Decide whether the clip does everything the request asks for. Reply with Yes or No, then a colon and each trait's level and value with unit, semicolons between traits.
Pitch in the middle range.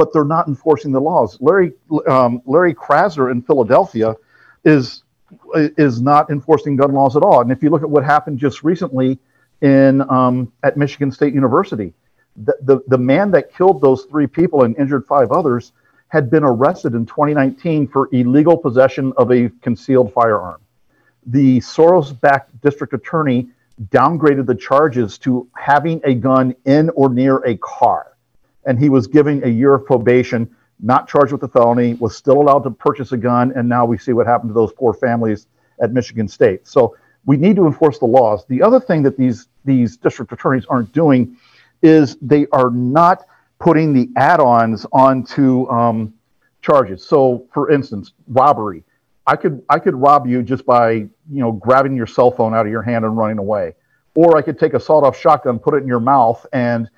No: low, 130 Hz